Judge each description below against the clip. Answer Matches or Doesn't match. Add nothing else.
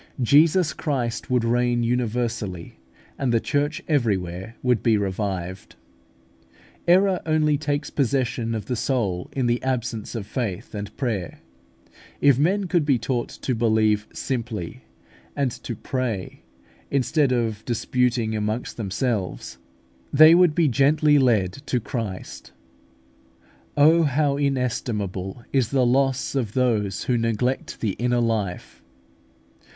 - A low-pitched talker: Matches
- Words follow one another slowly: Matches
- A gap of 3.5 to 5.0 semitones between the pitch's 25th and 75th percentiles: Matches